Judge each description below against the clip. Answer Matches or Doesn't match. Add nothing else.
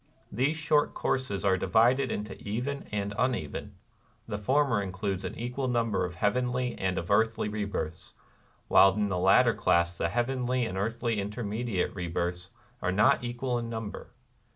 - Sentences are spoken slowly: Doesn't match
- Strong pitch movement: Doesn't match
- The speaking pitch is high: Doesn't match